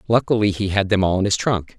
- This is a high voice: No, low, 100 Hz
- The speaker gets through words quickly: Yes, fast, 270 wpm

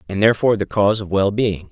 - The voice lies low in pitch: Yes, low, 100 Hz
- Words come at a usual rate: No, fast, 210 wpm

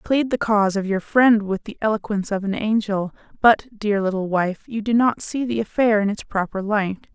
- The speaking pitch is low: No, high, 210 Hz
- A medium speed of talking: No, fast, 225 wpm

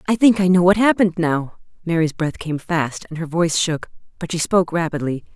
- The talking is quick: Yes, fast, 215 wpm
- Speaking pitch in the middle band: Yes, medium, 170 Hz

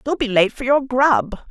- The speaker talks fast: Yes, fast, 240 wpm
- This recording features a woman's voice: Yes, female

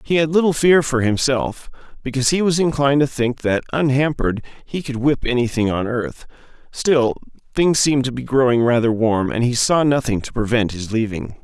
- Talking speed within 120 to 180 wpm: No, average, 190 wpm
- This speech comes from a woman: No, male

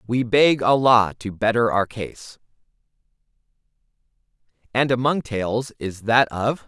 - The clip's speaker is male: Yes, male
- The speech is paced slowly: Yes, slow, 115 wpm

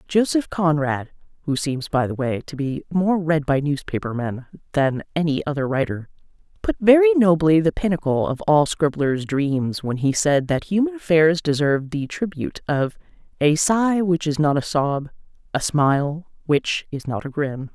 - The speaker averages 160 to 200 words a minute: Yes, average, 170 wpm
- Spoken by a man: No, female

